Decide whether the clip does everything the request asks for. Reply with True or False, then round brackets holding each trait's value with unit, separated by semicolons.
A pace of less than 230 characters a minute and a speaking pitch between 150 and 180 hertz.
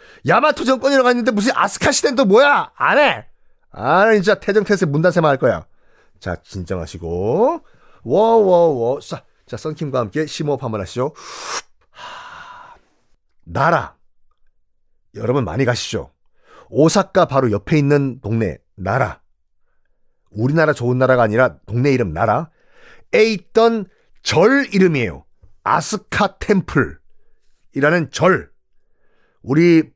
False (250 characters per minute; 165 Hz)